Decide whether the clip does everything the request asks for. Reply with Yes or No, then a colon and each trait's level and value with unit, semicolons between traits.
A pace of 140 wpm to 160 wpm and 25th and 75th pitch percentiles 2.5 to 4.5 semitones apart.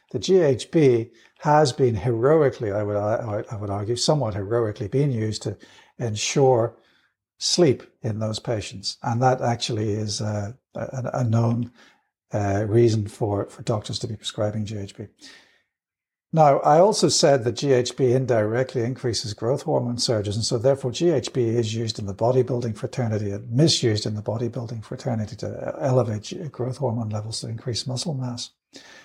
Yes: average, 150 wpm; average, 3.0 semitones